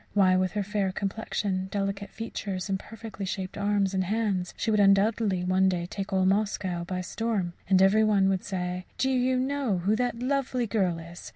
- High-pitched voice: Yes, high, 195 Hz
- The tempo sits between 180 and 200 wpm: Yes, average, 190 wpm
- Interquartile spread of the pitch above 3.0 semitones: No, average, 2.7 semitones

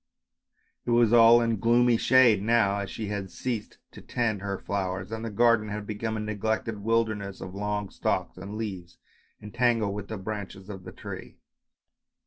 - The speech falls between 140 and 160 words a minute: No, average, 175 wpm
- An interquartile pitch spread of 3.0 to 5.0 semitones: No, narrow, 2.4 semitones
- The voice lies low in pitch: Yes, low, 105 Hz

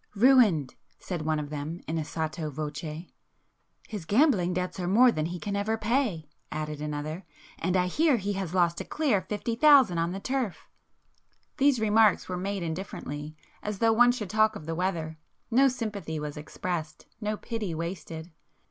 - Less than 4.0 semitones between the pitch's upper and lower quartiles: No, wide, 5.5 semitones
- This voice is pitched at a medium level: Yes, medium, 180 Hz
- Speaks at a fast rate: No, average, 160 wpm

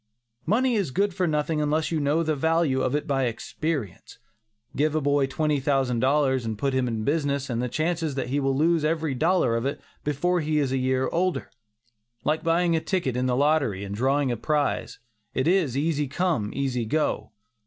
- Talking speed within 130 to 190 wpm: No, fast, 205 wpm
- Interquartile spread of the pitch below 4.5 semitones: Yes, average, 3.5 semitones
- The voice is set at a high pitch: No, medium, 145 Hz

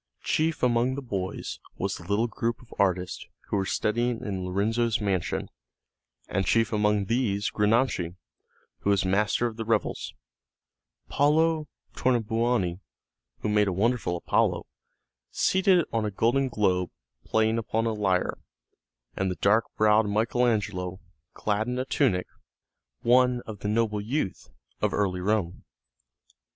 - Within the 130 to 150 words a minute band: Yes, average, 140 wpm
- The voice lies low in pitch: Yes, low, 110 Hz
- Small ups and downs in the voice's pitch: No, average, 3.3 semitones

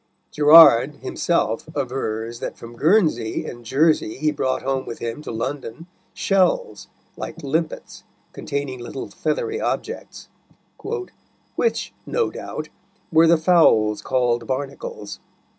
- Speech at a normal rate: No, slow, 115 wpm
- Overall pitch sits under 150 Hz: Yes, medium, 140 Hz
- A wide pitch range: Yes, wide, 5.7 semitones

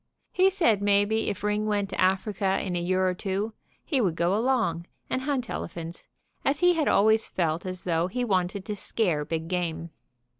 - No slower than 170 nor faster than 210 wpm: Yes, average, 190 wpm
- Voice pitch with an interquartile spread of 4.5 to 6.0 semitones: No, average, 3.9 semitones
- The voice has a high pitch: Yes, high, 195 Hz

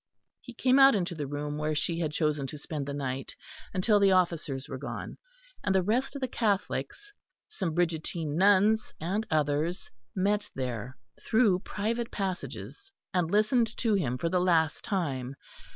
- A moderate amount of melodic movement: No, wide, 5.9 semitones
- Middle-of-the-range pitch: Yes, medium, 180 Hz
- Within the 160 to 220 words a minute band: Yes, average, 165 wpm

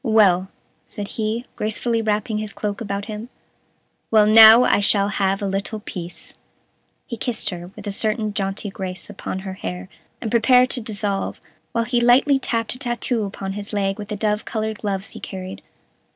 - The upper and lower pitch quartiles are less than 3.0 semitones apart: Yes, narrow, 2.4 semitones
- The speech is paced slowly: No, average, 180 wpm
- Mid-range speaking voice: No, high, 210 Hz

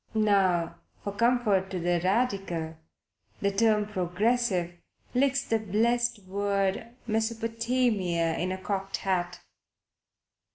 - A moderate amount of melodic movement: Yes, average, 3.7 semitones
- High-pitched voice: Yes, high, 200 Hz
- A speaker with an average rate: No, slow, 100 wpm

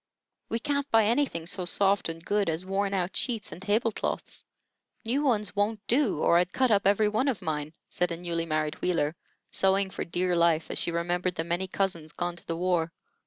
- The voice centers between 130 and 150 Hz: No, medium, 185 Hz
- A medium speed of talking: No, fast, 210 wpm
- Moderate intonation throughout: Yes, average, 3.7 semitones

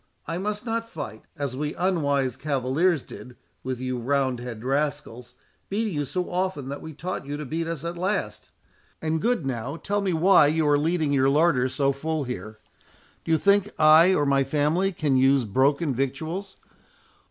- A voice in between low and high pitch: Yes, medium, 150 Hz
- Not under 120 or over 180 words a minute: Yes, average, 175 wpm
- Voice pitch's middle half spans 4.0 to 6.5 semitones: Yes, average, 4.4 semitones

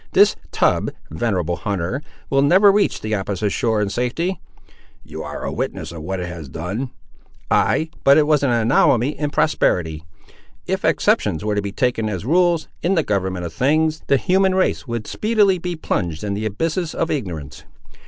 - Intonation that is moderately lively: No, wide, 8.8 semitones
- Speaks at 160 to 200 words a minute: Yes, average, 180 wpm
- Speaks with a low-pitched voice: Yes, low, 120 Hz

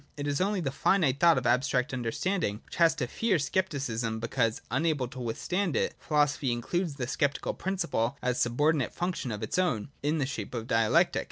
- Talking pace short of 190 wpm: No, average, 200 wpm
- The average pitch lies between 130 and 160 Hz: Yes, medium, 140 Hz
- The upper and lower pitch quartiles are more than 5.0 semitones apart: Yes, wide, 5.6 semitones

